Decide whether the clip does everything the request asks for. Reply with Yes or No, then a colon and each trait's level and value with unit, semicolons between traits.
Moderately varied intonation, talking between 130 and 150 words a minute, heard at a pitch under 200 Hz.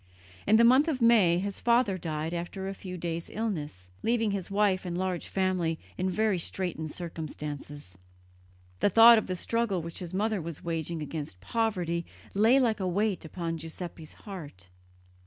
No: average, 4.4 semitones; average, 165 wpm; medium, 185 Hz